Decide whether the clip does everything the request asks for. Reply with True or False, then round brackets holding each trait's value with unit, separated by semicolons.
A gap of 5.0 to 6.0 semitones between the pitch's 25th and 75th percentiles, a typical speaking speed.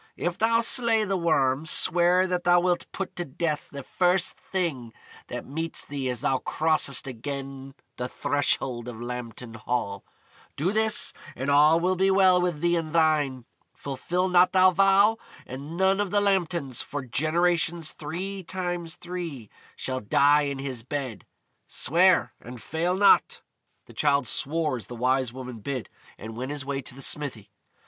True (5.4 semitones; 165 wpm)